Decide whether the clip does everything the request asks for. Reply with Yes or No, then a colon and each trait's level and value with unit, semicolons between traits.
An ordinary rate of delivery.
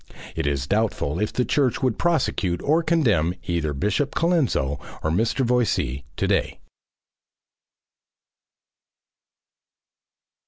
No: slow, 105 wpm